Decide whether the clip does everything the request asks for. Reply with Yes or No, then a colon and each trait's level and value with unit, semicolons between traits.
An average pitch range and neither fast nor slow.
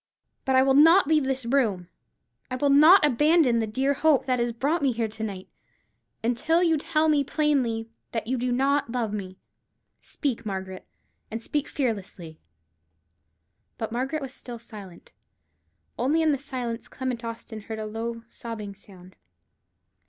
Yes: average, 4.1 semitones; average, 160 wpm